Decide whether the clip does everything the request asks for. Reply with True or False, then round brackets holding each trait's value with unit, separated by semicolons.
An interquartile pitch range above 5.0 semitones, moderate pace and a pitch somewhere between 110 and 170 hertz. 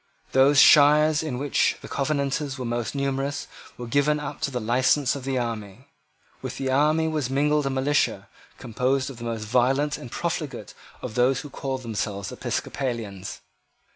False (3.2 semitones; 165 wpm; 135 Hz)